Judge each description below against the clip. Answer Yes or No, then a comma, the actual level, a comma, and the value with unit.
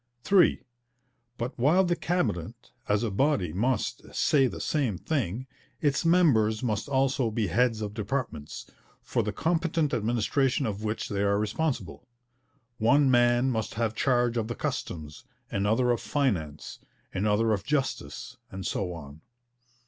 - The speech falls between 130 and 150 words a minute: Yes, average, 140 wpm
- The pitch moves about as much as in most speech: Yes, average, 4.8 semitones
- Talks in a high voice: No, low, 120 Hz